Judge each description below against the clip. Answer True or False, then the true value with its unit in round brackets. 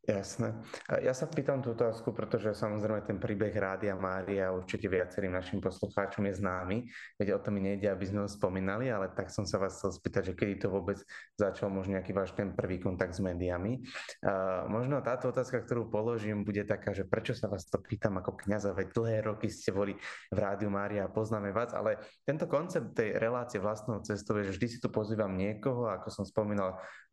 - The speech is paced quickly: True (200 wpm)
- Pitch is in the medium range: False (105 Hz)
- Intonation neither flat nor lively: False (2.3 semitones)